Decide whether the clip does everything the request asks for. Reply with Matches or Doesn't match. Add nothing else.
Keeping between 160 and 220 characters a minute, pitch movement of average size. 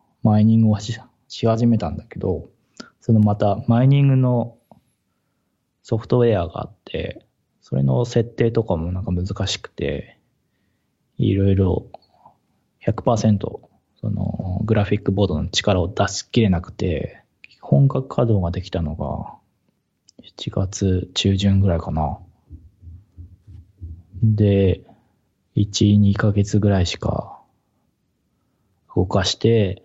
Matches